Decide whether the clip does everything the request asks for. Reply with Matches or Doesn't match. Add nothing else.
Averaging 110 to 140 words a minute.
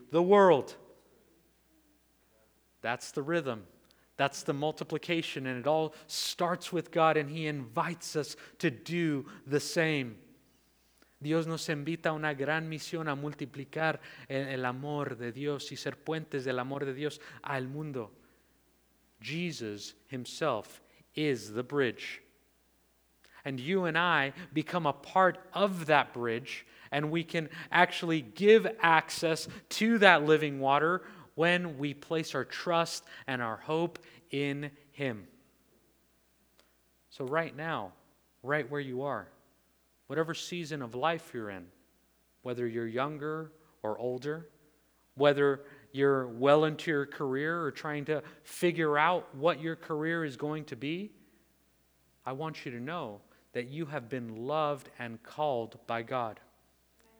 Matches